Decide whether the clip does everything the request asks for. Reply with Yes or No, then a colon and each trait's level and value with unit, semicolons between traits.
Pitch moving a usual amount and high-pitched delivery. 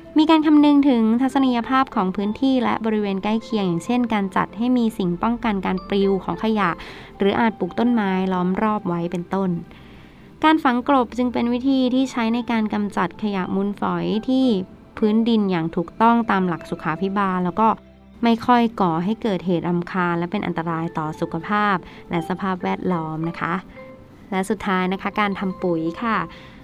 Yes: average, 4.3 semitones; high, 200 Hz